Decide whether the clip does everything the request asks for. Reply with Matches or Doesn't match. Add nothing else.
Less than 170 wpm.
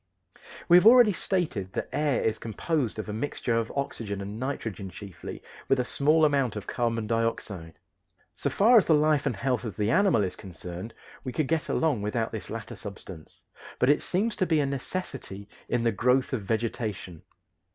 Doesn't match